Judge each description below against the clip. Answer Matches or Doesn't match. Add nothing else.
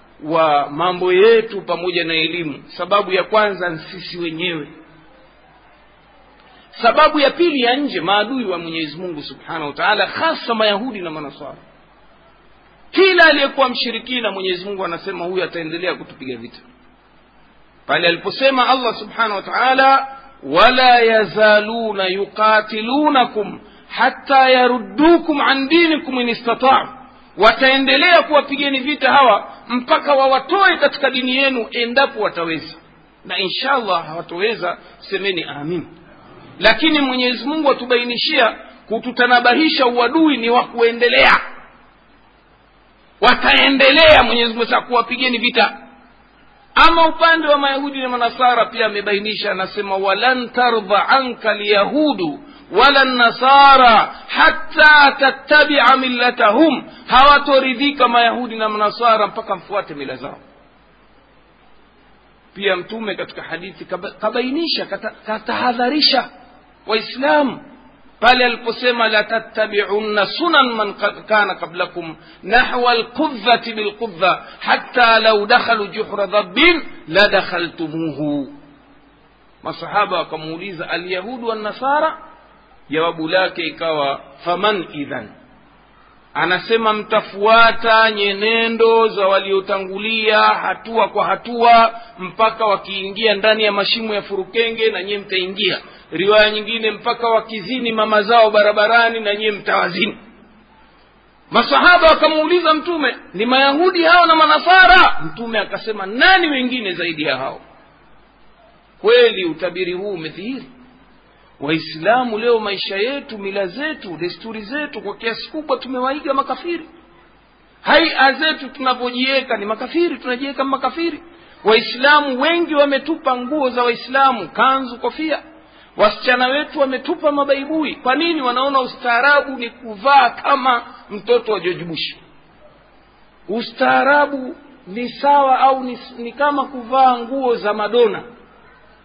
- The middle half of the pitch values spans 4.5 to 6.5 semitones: Matches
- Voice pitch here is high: Matches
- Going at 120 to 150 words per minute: Doesn't match